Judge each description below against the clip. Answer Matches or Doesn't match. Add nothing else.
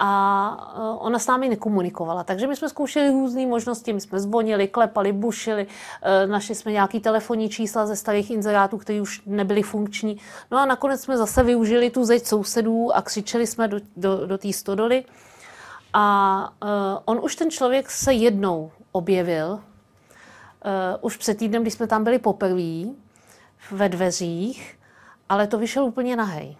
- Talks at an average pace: Matches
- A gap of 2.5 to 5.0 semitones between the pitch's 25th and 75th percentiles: Matches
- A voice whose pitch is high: Matches